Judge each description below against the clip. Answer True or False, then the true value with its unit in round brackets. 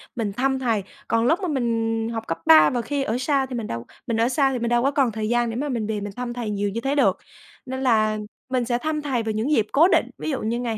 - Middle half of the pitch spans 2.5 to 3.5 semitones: True (3.2 semitones)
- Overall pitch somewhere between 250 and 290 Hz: False (240 Hz)